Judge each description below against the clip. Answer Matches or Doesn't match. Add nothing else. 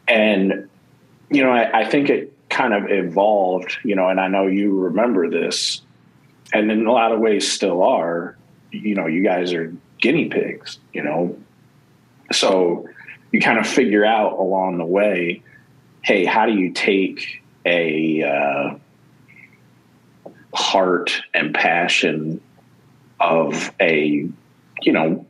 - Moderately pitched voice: Doesn't match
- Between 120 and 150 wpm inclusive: Matches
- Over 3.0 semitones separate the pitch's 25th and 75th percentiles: Matches